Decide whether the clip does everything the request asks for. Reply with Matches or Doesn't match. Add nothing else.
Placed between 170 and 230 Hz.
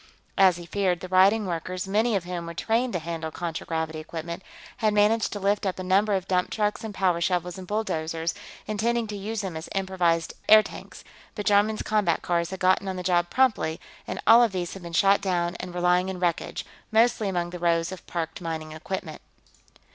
Matches